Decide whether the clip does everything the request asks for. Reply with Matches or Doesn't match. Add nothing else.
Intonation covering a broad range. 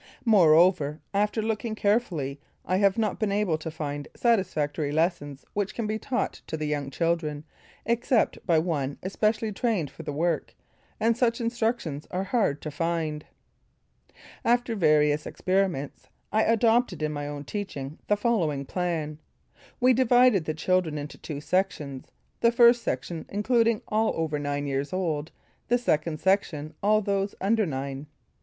Matches